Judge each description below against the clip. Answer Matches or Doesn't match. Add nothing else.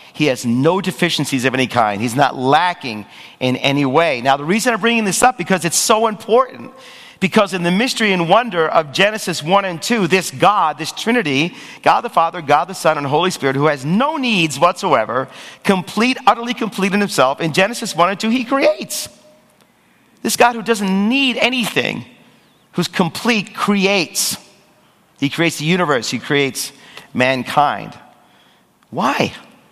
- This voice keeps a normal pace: Matches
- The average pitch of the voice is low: Doesn't match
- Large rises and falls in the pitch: Matches